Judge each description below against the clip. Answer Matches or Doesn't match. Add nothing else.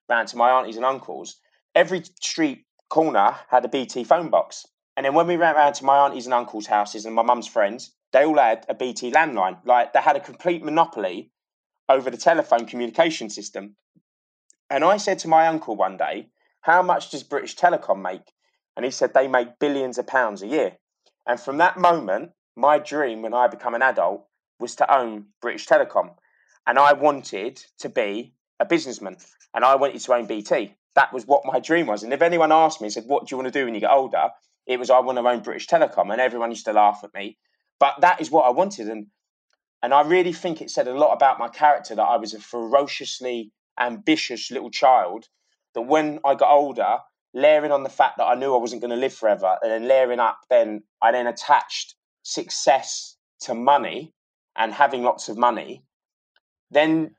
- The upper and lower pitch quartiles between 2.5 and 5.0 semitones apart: Matches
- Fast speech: Matches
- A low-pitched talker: Matches